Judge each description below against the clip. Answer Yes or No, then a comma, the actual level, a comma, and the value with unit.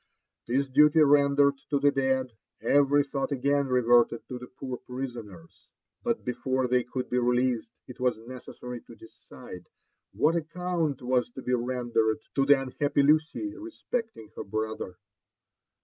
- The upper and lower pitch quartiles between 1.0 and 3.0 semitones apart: Yes, average, 2.7 semitones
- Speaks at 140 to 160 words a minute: Yes, average, 150 wpm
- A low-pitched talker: Yes, low, 130 Hz